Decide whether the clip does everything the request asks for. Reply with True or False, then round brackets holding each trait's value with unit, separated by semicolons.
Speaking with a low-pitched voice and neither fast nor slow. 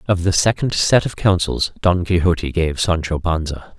True (90 Hz; 175 wpm)